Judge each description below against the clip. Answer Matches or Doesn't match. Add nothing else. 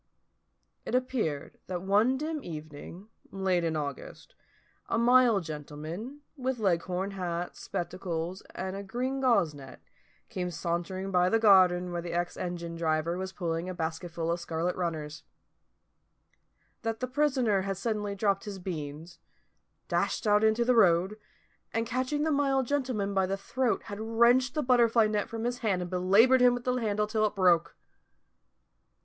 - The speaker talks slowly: Doesn't match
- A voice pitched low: Doesn't match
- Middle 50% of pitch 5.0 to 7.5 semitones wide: Matches